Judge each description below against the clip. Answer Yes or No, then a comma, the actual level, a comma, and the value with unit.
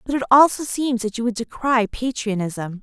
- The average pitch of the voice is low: No, high, 235 Hz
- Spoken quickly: No, average, 190 wpm